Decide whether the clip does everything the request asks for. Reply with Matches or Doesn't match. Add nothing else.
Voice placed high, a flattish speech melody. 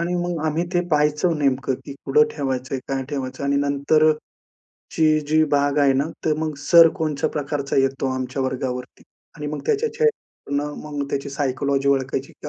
Doesn't match